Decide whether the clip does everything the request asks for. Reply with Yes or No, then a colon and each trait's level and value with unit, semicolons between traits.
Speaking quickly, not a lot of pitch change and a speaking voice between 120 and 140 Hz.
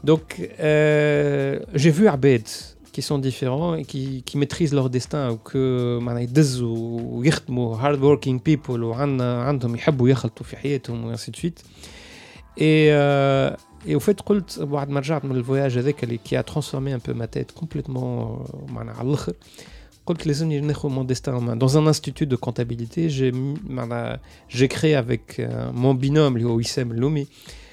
No: fast, 160 wpm; average, 3.3 semitones; low, 135 Hz